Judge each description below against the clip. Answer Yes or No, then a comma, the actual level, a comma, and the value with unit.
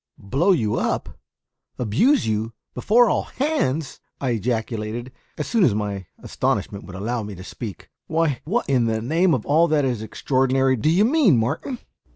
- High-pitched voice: No, low, 130 Hz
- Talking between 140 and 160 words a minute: No, average, 170 wpm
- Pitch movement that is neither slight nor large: No, wide, 6.9 semitones